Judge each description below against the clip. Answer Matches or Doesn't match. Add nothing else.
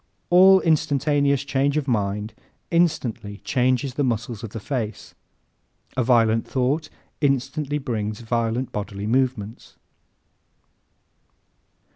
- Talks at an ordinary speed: Doesn't match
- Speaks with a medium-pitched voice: Doesn't match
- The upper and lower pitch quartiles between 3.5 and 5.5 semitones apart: Matches